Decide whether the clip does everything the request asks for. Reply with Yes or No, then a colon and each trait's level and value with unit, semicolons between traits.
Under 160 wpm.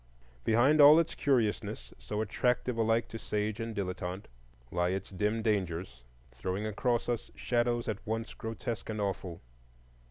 Yes: average, 140 wpm